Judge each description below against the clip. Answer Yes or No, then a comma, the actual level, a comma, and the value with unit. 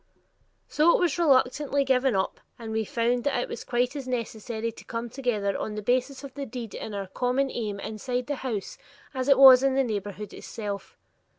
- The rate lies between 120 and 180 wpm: No, average, 200 wpm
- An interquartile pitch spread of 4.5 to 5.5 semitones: No, average, 3.6 semitones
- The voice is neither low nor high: No, high, 245 Hz